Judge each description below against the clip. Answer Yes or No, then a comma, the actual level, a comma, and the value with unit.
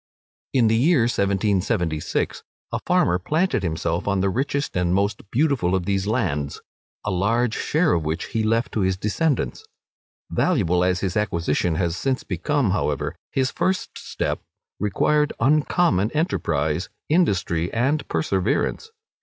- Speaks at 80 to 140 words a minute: Yes, slow, 135 wpm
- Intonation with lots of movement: Yes, wide, 7.0 semitones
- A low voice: Yes, low, 100 Hz